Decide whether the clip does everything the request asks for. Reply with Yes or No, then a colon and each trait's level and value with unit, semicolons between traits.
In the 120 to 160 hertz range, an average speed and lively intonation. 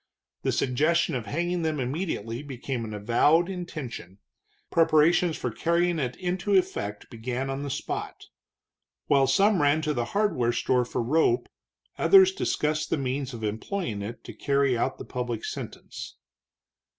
Yes: medium, 140 Hz; average, 150 wpm; wide, 5.8 semitones